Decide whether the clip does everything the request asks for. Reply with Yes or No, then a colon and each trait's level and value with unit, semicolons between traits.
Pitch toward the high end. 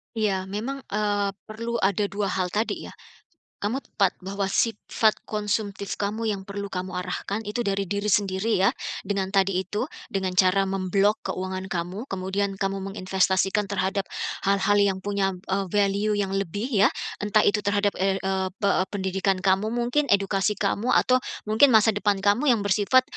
Yes: high, 200 Hz